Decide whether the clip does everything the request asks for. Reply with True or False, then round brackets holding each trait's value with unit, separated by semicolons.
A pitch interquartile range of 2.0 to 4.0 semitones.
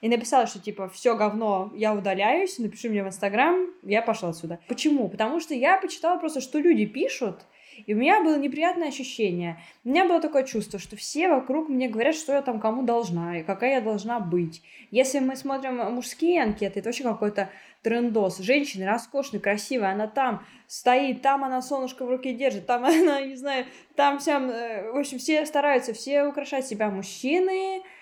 False (5.1 semitones)